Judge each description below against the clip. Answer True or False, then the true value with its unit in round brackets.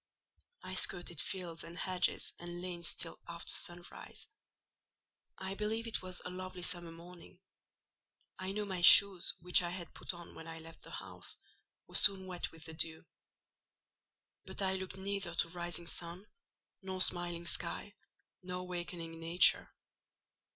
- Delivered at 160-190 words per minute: False (145 wpm)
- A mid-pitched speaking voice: True (175 Hz)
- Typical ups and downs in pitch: False (1.6 semitones)